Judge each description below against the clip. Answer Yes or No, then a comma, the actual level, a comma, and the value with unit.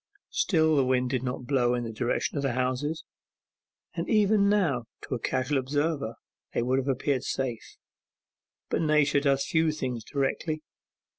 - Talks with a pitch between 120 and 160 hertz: Yes, low, 135 Hz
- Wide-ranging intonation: No, average, 3.4 semitones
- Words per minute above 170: No, average, 160 wpm